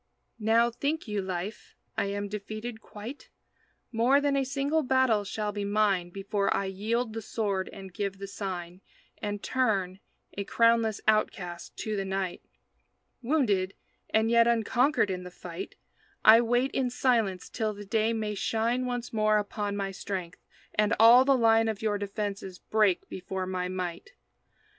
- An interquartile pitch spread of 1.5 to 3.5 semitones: Yes, average, 3.0 semitones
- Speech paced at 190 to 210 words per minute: No, average, 155 wpm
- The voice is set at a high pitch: Yes, high, 210 Hz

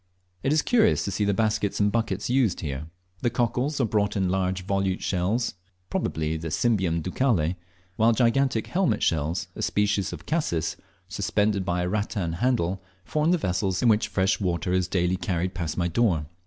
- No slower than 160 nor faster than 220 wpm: Yes, average, 180 wpm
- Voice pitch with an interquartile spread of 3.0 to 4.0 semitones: No, average, 4.7 semitones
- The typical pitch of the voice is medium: No, low, 100 Hz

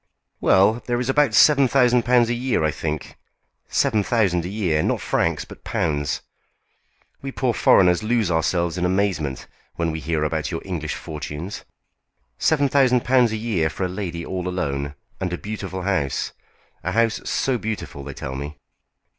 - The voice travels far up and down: Yes, wide, 6.9 semitones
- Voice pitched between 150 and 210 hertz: No, very low, 95 Hz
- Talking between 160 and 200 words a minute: Yes, average, 170 wpm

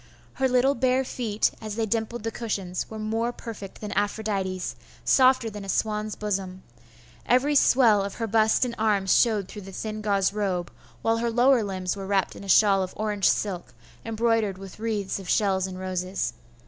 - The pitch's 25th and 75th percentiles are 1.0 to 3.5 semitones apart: Yes, average, 2.7 semitones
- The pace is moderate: Yes, average, 185 wpm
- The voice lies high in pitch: Yes, high, 210 Hz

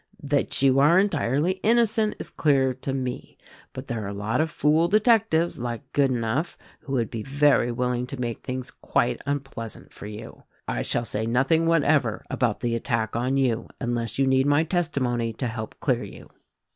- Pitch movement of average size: Yes, average, 4.1 semitones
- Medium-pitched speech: No, low, 130 Hz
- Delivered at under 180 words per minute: No, average, 185 wpm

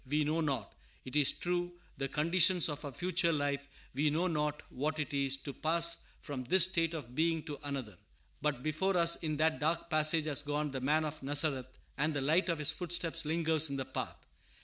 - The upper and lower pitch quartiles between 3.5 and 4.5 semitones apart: No, narrow, 2.6 semitones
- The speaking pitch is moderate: Yes, medium, 155 Hz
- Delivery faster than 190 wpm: Yes, fast, 205 wpm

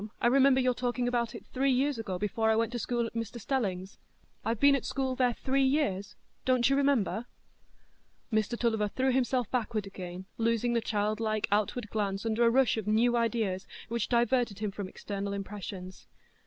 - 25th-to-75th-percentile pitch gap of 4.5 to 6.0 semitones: No, average, 3.2 semitones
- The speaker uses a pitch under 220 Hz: No, high, 230 Hz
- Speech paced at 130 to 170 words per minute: No, average, 180 wpm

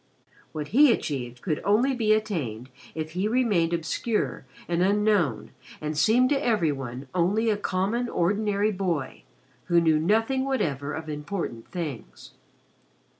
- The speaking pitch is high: No, medium, 180 Hz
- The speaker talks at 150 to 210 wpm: No, slow, 135 wpm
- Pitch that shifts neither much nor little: No, wide, 6.2 semitones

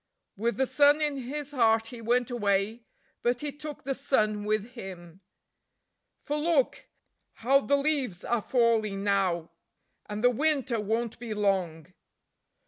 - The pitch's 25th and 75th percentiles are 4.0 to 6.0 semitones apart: Yes, average, 4.7 semitones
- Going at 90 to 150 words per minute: Yes, average, 140 wpm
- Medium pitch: No, high, 235 Hz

